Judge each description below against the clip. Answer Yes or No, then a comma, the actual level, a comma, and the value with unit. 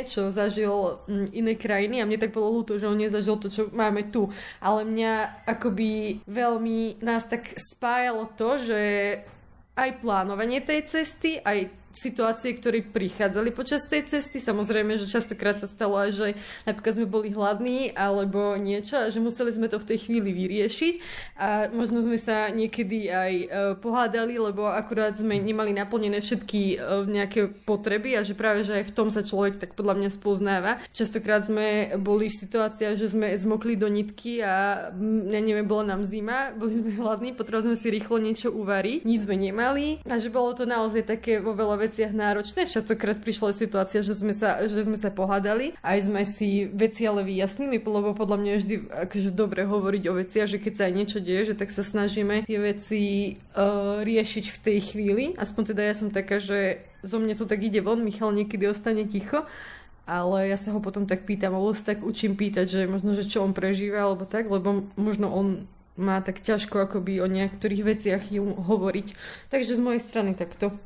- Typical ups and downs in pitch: No, narrow, 1.8 semitones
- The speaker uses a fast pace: Yes, fast, 185 wpm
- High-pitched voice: Yes, high, 210 Hz